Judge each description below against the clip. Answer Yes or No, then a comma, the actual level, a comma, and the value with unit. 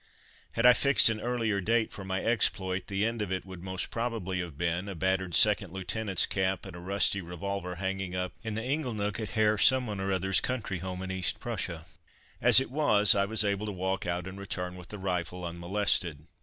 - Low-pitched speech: Yes, very low, 95 Hz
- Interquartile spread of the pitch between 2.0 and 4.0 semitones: Yes, average, 2.9 semitones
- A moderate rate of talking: No, fast, 210 wpm